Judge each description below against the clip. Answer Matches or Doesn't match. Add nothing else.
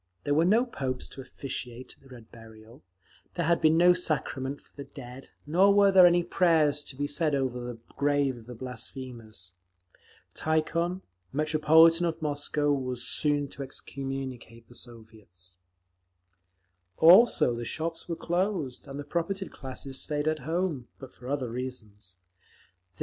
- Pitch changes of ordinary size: Matches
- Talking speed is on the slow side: Doesn't match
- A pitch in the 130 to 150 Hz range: Matches